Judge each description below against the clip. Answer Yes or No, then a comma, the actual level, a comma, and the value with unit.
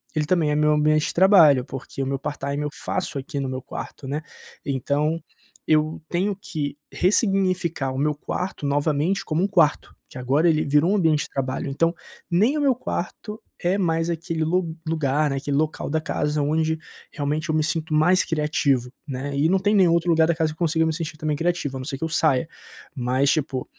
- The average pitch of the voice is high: No, medium, 155 Hz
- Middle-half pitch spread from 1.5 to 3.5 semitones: Yes, average, 2.9 semitones